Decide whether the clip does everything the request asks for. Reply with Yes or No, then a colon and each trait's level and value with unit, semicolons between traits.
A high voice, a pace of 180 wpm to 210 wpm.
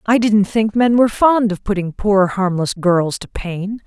Yes: high, 205 Hz; average, 200 wpm